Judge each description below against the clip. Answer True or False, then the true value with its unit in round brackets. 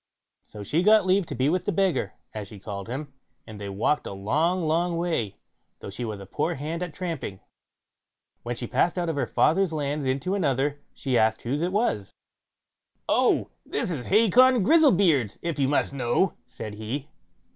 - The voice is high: False (145 Hz)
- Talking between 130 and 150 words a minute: False (190 wpm)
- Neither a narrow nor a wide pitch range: False (7.2 semitones)